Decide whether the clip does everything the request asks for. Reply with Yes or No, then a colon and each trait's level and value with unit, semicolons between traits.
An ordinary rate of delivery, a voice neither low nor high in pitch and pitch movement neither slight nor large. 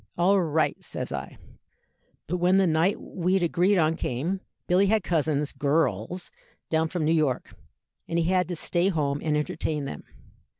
Yes: average, 165 wpm; medium, 165 Hz; average, 3.2 semitones